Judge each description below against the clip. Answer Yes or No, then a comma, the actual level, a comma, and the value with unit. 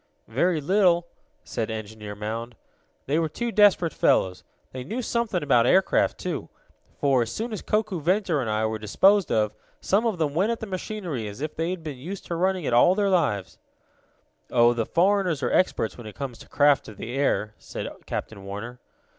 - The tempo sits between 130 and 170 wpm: No, average, 190 wpm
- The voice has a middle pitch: Yes, medium, 150 Hz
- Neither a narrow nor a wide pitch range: No, wide, 8.6 semitones